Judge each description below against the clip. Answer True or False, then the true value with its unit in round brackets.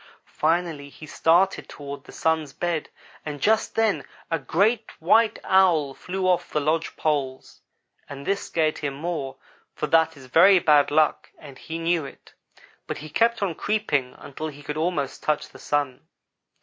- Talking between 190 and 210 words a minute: False (170 wpm)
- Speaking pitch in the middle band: True (155 Hz)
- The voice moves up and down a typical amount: True (3.7 semitones)